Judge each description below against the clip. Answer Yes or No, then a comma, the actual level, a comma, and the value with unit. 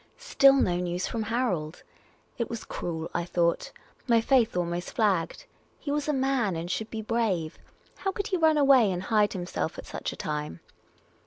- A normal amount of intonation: No, wide, 7.0 semitones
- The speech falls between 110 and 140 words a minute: No, average, 180 wpm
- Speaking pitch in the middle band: No, high, 215 Hz